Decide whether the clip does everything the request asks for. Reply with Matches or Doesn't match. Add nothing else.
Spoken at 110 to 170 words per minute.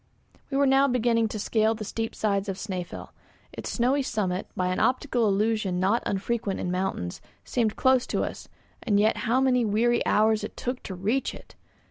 Doesn't match